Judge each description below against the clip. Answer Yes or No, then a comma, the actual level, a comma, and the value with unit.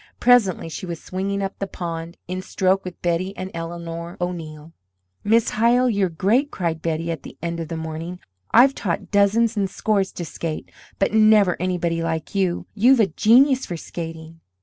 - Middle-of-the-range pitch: Yes, medium, 180 Hz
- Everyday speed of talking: Yes, average, 175 wpm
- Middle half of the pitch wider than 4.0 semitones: No, average, 3.5 semitones